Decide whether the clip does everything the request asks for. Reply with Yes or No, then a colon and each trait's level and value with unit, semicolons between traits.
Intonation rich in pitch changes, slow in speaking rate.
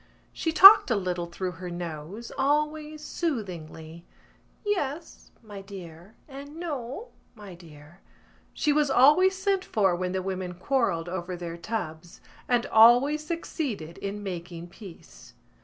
Yes: wide, 8.9 semitones; slow, 130 wpm